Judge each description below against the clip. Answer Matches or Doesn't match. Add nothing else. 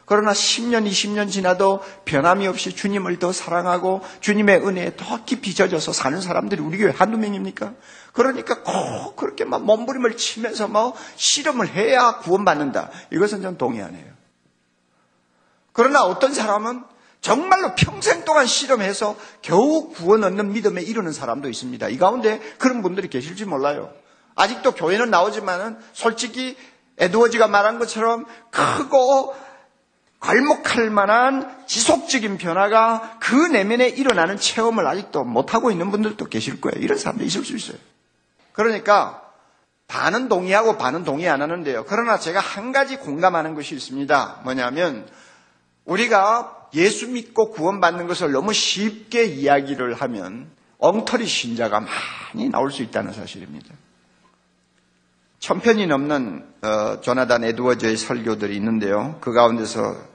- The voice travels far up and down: Matches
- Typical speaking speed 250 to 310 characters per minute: Doesn't match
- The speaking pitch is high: Matches